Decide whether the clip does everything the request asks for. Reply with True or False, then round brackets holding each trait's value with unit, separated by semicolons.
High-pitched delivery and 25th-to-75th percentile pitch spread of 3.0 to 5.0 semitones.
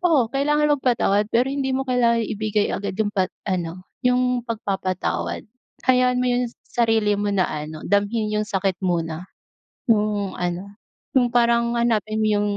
True (215 Hz; 4.0 semitones)